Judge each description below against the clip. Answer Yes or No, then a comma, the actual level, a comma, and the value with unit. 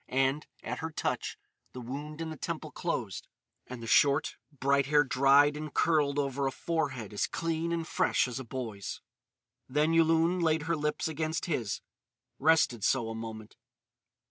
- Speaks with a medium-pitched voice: Yes, medium, 145 Hz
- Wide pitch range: No, average, 3.7 semitones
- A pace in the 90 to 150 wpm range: No, average, 165 wpm